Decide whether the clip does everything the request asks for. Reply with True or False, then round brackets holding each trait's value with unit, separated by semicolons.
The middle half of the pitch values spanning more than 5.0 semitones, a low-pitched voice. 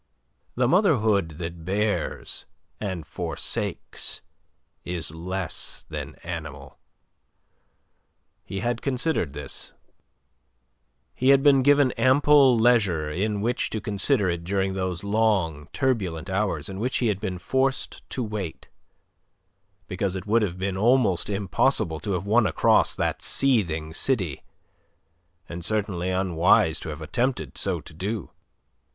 True (5.6 semitones; 100 Hz)